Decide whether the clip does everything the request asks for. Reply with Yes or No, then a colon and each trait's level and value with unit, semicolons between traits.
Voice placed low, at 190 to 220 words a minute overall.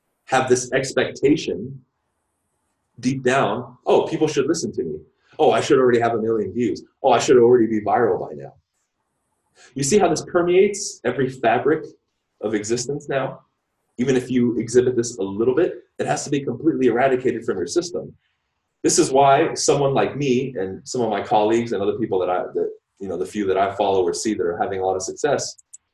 Yes: low, 130 Hz; average, 200 wpm